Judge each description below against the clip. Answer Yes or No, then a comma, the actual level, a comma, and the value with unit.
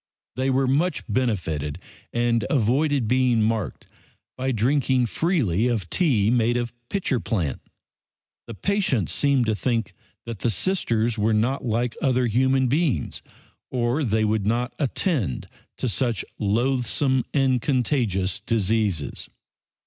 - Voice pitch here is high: No, low, 120 Hz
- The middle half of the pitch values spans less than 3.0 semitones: No, average, 3.4 semitones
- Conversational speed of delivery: No, slow, 125 wpm